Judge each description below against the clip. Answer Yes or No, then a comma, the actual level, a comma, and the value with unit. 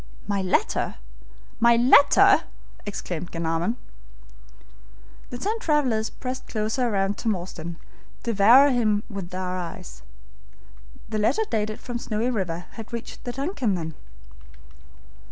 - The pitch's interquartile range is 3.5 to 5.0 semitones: Yes, average, 4.7 semitones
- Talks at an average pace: No, slow, 120 wpm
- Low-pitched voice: No, high, 215 Hz